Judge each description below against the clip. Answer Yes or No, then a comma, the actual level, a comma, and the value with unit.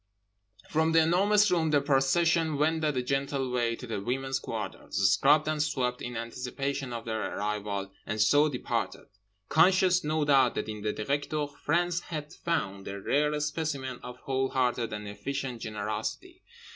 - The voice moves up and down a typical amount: Yes, average, 4.7 semitones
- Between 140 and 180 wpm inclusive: Yes, average, 150 wpm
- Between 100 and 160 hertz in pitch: Yes, low, 135 Hz